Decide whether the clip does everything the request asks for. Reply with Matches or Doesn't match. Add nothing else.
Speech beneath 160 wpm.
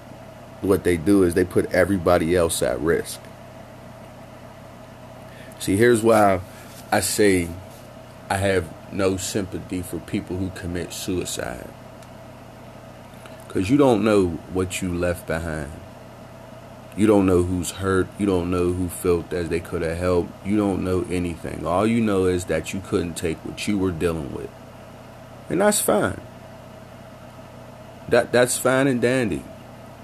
Matches